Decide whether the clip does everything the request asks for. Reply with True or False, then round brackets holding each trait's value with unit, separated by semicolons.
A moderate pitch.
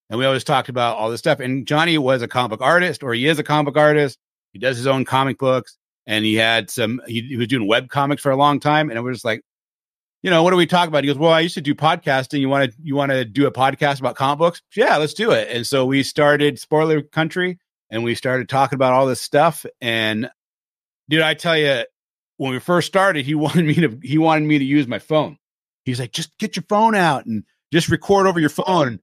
True (145 Hz)